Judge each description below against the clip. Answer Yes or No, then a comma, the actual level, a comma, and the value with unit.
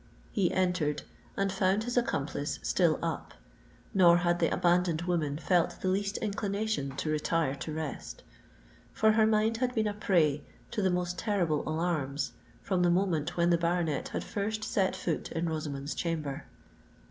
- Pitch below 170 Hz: No, medium, 175 Hz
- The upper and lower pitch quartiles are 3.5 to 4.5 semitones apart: Yes, average, 4.1 semitones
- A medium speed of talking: Yes, average, 160 wpm